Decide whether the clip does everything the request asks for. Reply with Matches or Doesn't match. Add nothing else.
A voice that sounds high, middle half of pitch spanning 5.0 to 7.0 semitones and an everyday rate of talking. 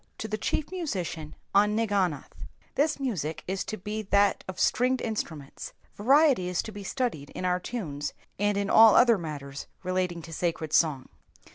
Matches